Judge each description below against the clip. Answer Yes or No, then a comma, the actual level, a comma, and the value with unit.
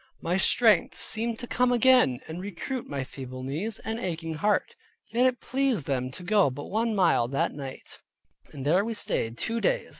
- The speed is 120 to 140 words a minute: No, average, 185 wpm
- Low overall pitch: No, high, 190 Hz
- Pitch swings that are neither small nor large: No, wide, 8.5 semitones